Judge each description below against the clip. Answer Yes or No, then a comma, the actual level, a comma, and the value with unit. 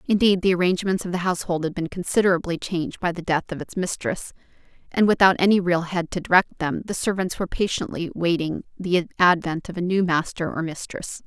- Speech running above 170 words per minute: Yes, average, 195 wpm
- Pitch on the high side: No, medium, 180 Hz